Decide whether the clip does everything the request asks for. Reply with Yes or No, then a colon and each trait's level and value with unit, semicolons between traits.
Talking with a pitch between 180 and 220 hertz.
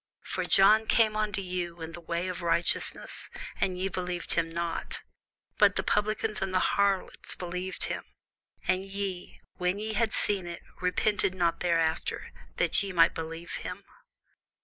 Yes: medium, 185 Hz